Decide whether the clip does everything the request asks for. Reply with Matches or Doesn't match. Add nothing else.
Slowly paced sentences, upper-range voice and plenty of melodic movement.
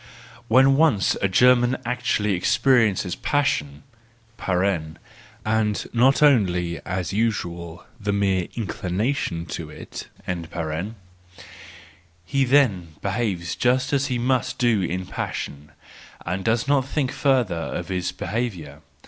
Doesn't match